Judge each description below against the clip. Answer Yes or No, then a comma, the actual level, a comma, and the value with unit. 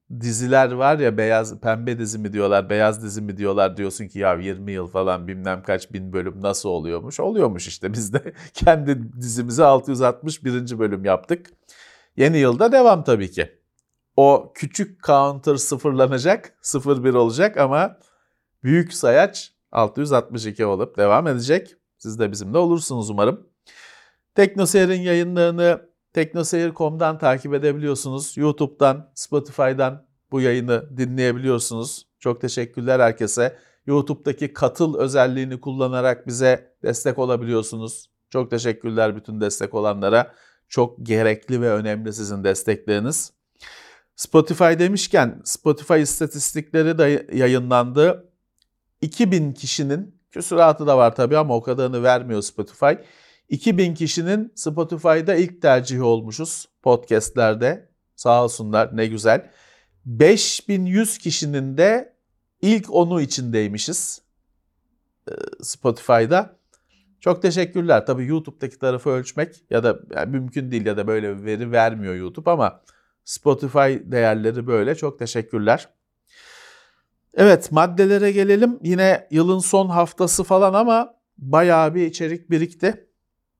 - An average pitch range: No, wide, 6.5 semitones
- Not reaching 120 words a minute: Yes, average, 110 wpm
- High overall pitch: No, low, 135 Hz